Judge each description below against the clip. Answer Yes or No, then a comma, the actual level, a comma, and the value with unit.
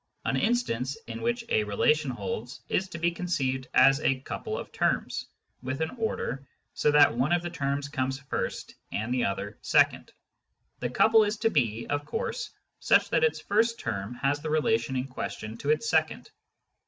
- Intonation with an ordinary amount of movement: No, wide, 5.7 semitones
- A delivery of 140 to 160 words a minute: No, average, 190 wpm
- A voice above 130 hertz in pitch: Yes, medium, 140 Hz